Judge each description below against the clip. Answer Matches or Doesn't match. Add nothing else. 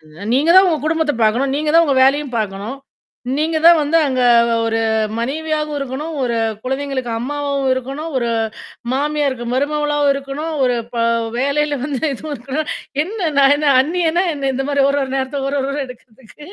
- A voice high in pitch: Matches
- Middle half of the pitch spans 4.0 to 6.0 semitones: Doesn't match